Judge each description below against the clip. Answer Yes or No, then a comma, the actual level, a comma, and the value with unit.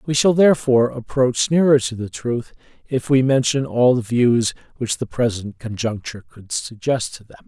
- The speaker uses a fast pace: No, average, 175 wpm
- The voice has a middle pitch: No, low, 120 Hz